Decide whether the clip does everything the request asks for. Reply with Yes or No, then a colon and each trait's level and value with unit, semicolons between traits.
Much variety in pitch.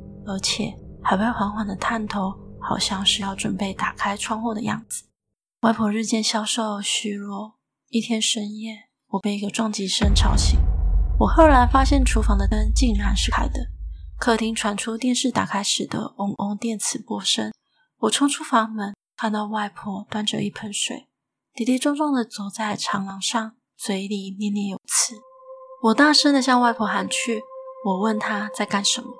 No: average, 2.9 semitones